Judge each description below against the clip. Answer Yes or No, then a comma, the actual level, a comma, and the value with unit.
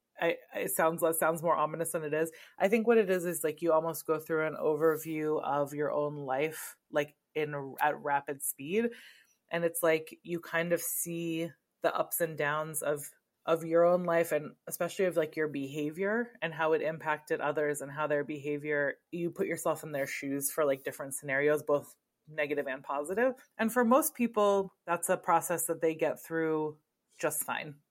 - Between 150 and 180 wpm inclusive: No, average, 190 wpm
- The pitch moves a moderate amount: No, narrow, 2.3 semitones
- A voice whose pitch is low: No, medium, 160 Hz